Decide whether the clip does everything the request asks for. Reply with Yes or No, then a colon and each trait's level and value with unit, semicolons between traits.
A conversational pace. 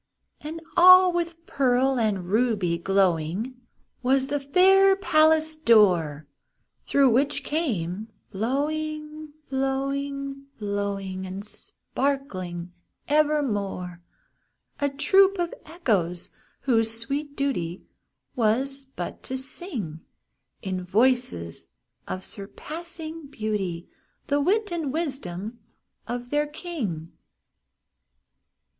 No: slow, 90 wpm